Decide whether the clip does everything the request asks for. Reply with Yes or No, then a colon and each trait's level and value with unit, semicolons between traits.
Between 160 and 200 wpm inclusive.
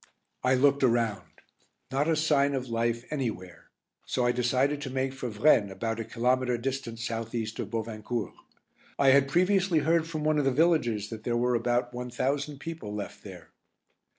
Yes: average, 180 wpm